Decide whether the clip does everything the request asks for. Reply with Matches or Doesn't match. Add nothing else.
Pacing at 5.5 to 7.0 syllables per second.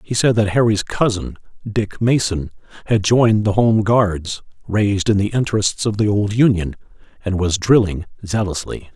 Doesn't match